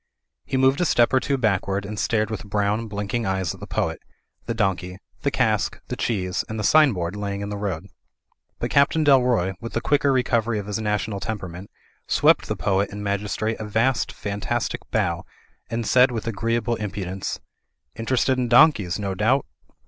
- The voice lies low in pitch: Yes, low, 105 Hz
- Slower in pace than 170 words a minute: No, average, 185 wpm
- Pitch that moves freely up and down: No, average, 3.2 semitones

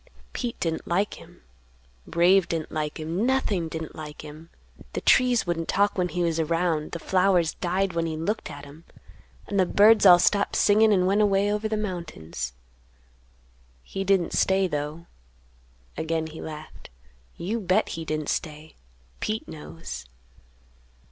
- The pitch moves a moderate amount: Yes, average, 3.9 semitones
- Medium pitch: Yes, medium, 175 Hz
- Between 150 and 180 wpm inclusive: Yes, average, 155 wpm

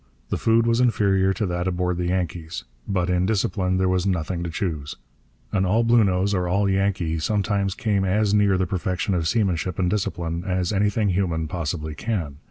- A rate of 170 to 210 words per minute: Yes, average, 180 wpm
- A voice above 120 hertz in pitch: No, very low, 95 Hz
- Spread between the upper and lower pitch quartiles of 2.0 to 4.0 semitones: Yes, narrow, 2.5 semitones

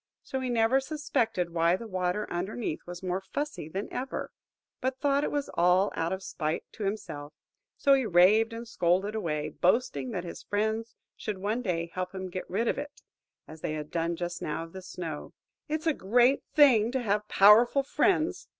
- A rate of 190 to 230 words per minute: Yes, average, 195 wpm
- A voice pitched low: No, high, 205 Hz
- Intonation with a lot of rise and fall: Yes, wide, 5.8 semitones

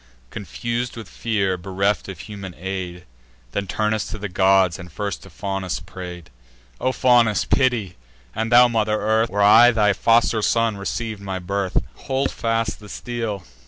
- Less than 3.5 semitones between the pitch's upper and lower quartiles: Yes, average, 3.1 semitones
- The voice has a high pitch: No, low, 105 Hz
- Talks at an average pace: Yes, average, 160 wpm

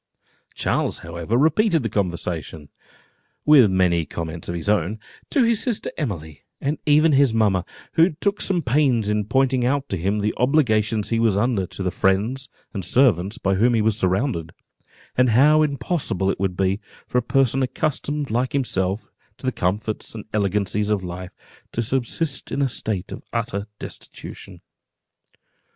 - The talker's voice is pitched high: No, low, 110 Hz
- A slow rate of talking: No, average, 165 wpm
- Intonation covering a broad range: Yes, wide, 6.0 semitones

